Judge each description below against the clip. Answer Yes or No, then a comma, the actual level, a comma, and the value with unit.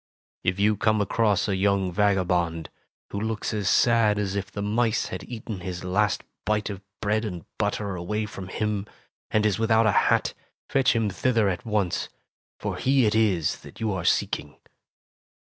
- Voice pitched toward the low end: Yes, low, 105 Hz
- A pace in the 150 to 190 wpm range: Yes, average, 175 wpm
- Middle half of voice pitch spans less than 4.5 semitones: Yes, narrow, 2.5 semitones